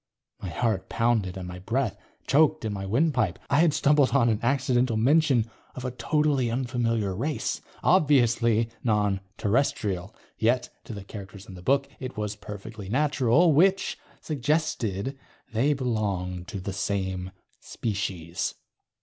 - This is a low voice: Yes, low, 115 Hz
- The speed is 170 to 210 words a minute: No, average, 140 wpm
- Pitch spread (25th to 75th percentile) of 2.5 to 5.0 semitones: No, wide, 5.5 semitones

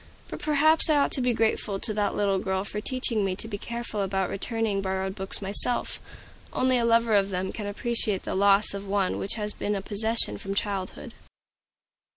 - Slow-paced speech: No, average, 195 wpm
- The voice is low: No, high, 205 Hz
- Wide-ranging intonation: No, average, 2.9 semitones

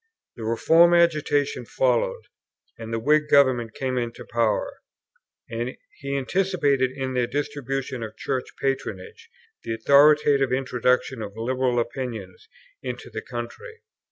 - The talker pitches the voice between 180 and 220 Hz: No, low, 130 Hz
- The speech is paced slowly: Yes, slow, 125 wpm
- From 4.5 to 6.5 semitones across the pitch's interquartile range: No, average, 3.4 semitones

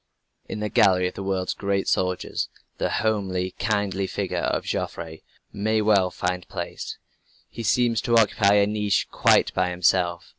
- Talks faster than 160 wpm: No, average, 155 wpm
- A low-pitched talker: Yes, low, 100 Hz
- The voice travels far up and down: No, narrow, 2.6 semitones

